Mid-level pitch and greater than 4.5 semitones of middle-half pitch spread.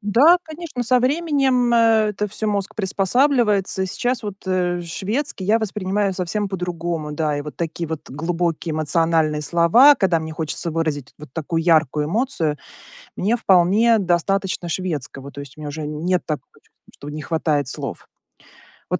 Yes: medium, 180 Hz; average, 5.3 semitones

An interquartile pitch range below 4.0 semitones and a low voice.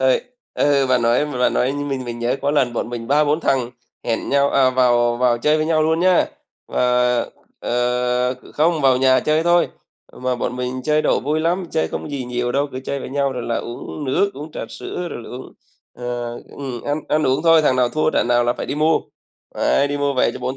Yes: average, 3.4 semitones; low, 130 Hz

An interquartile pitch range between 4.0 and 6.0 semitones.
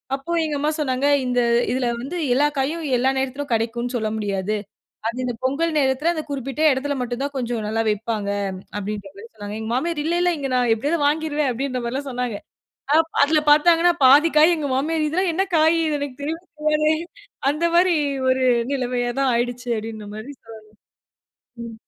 Yes: average, 4.3 semitones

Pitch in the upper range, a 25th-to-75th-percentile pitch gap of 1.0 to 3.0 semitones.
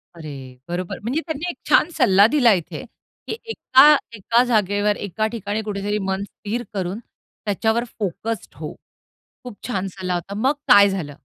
No: high, 205 Hz; average, 3.7 semitones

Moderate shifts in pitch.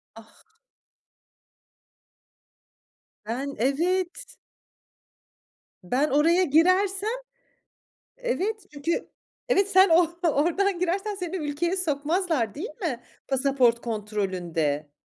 No: wide, 7.0 semitones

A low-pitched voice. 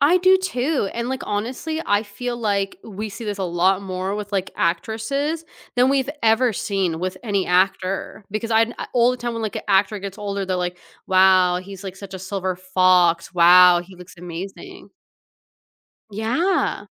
No: high, 200 Hz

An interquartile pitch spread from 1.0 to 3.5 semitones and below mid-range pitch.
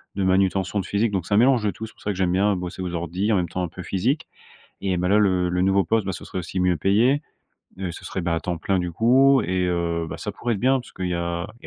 Yes: average, 2.8 semitones; very low, 95 Hz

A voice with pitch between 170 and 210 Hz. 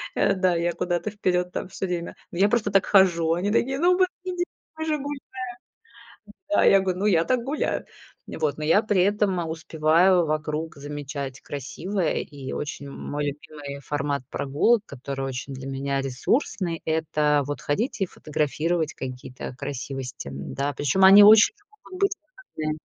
No: medium, 160 Hz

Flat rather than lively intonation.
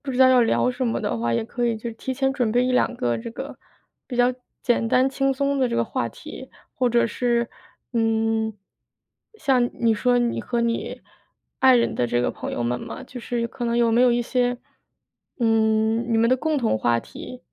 Yes: narrow, 2.0 semitones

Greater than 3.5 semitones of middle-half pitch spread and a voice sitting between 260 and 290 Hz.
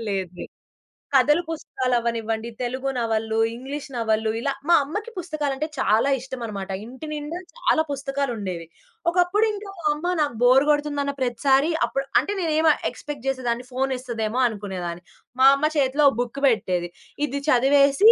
Yes: average, 4.3 semitones; very high, 265 Hz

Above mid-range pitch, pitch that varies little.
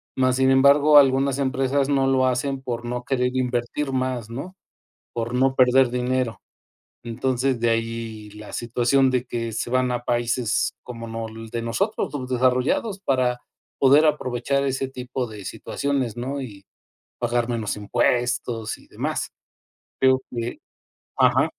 No: low, 125 Hz; narrow, 2.1 semitones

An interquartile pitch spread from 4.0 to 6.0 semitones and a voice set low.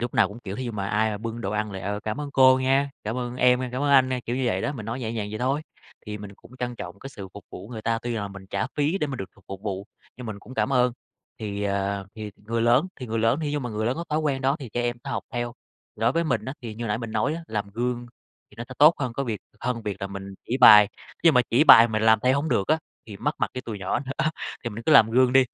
No: average, 3.6 semitones; low, 115 Hz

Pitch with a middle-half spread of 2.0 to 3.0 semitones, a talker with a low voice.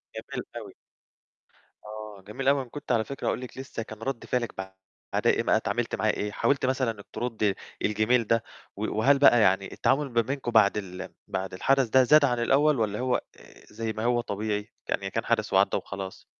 No: average, 3.7 semitones; low, 115 Hz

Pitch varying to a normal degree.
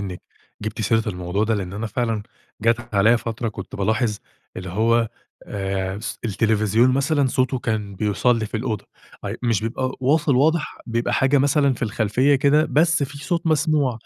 Yes: average, 4.1 semitones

